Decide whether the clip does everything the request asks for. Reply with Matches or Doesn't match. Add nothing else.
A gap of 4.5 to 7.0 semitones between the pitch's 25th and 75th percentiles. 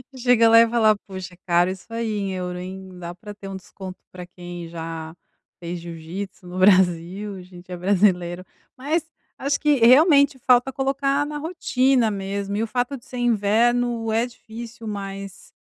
Matches